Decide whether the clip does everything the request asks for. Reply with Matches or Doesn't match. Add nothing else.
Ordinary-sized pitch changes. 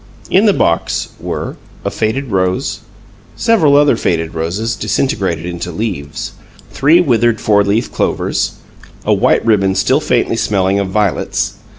Doesn't match